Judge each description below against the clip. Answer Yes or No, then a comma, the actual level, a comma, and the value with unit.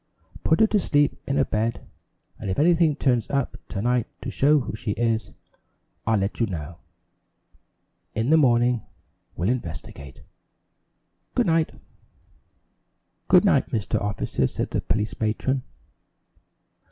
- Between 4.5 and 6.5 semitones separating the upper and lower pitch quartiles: Yes, average, 4.9 semitones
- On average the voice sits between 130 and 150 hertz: No, low, 120 Hz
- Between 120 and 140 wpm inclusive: Yes, slow, 135 wpm